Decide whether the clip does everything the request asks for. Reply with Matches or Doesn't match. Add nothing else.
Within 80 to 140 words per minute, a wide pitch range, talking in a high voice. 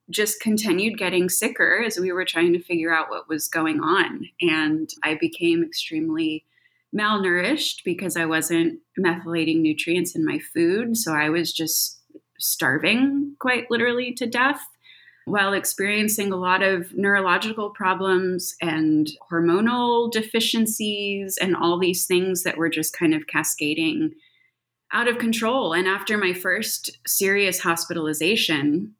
Matches